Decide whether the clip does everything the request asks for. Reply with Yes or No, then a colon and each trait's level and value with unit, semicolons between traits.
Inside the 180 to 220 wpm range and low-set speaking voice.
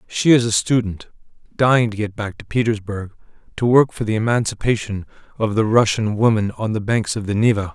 Yes: average, 195 wpm; low, 110 Hz